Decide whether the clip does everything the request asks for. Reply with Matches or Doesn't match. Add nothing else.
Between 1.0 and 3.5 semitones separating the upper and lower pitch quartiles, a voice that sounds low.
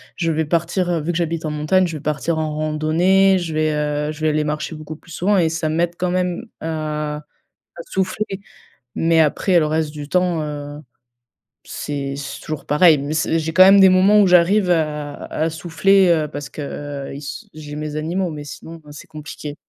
Doesn't match